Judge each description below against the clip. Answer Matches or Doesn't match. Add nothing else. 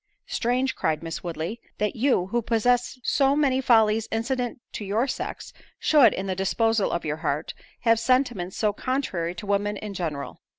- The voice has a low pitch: Doesn't match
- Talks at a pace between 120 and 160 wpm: Doesn't match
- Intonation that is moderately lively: Matches